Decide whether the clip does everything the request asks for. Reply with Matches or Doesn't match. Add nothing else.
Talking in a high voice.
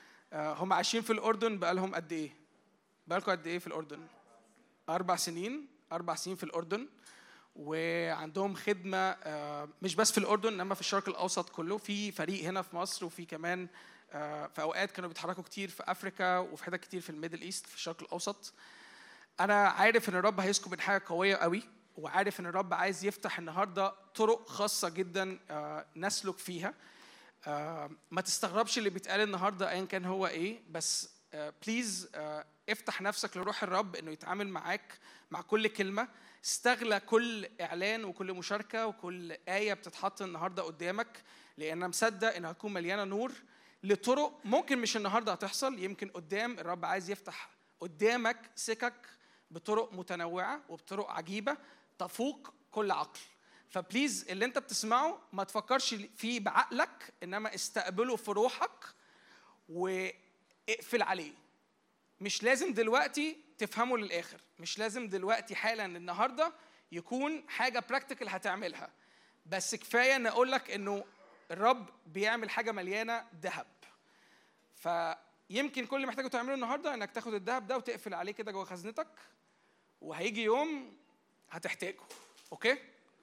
Matches